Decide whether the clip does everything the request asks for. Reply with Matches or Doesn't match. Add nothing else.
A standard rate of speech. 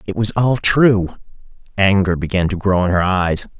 Matches